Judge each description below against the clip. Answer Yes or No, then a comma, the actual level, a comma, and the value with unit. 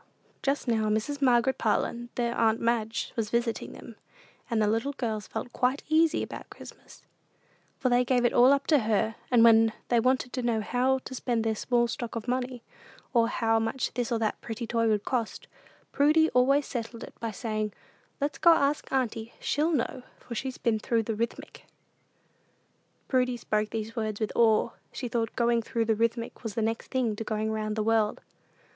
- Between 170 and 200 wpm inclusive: Yes, average, 190 wpm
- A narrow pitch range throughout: Yes, narrow, 2.2 semitones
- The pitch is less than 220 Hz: No, high, 235 Hz